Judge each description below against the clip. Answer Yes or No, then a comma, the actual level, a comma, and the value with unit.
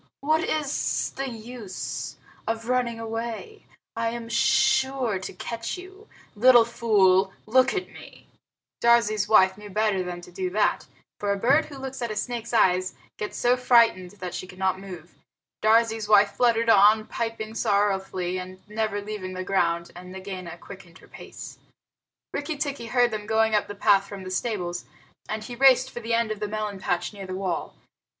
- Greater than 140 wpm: Yes, average, 175 wpm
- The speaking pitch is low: No, high, 215 Hz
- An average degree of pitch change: Yes, average, 3.8 semitones